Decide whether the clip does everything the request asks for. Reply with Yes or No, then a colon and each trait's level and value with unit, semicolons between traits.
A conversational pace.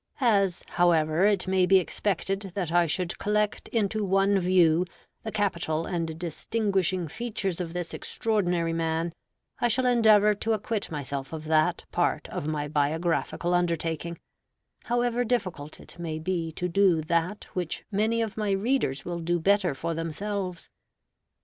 Yes: average, 150 wpm